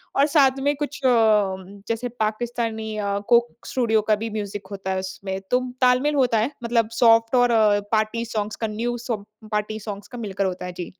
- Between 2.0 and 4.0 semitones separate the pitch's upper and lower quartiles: Yes, average, 2.8 semitones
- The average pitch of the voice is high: Yes, high, 225 Hz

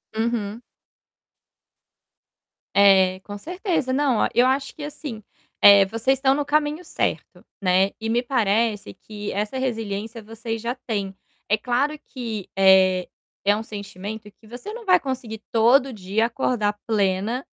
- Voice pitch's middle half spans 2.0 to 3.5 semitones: No, average, 4.3 semitones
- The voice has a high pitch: Yes, high, 225 Hz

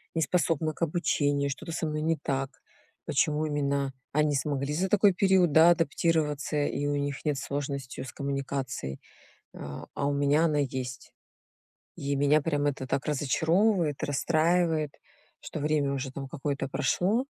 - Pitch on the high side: No, medium, 145 Hz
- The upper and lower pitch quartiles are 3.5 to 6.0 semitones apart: No, narrow, 2.5 semitones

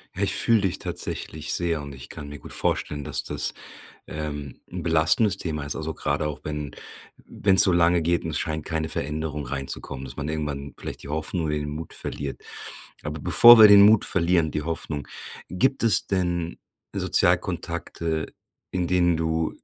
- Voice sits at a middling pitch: No, very low, 80 Hz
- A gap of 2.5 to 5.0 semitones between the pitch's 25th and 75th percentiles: Yes, average, 2.8 semitones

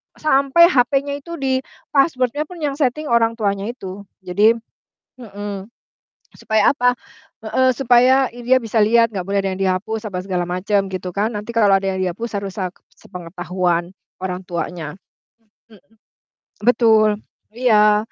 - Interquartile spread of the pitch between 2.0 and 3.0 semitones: No, average, 4.4 semitones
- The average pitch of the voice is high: Yes, high, 215 Hz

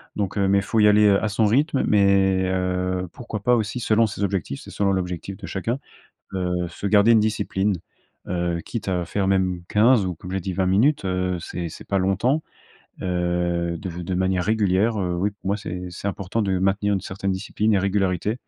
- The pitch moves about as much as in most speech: No, narrow, 2.3 semitones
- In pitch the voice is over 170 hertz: No, very low, 95 Hz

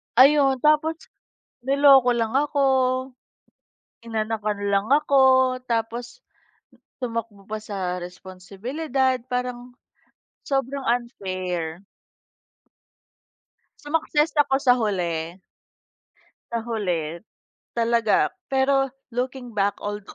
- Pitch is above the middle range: Yes, high, 235 Hz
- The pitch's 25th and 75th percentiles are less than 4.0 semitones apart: No, average, 4.8 semitones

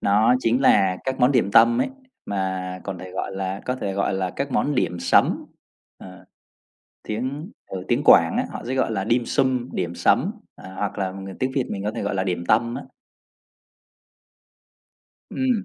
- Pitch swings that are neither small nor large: Yes, average, 5.0 semitones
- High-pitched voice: No, low, 100 Hz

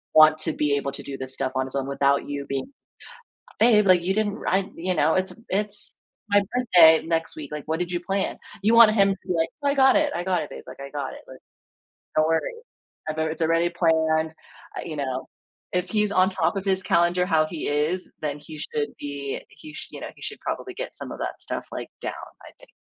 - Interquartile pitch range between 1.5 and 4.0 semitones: No, average, 4.6 semitones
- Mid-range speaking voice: Yes, medium, 165 Hz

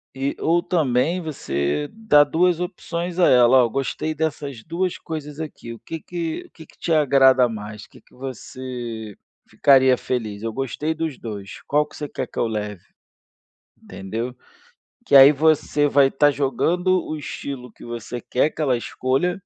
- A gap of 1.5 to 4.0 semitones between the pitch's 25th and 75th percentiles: No, average, 4.6 semitones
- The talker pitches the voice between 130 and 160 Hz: Yes, medium, 140 Hz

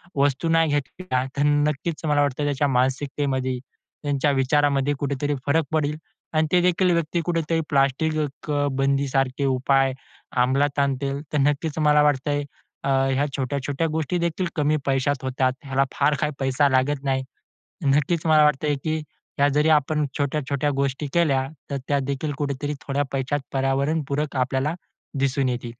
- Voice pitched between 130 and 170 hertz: Yes, medium, 140 Hz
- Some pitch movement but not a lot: No, narrow, 1.9 semitones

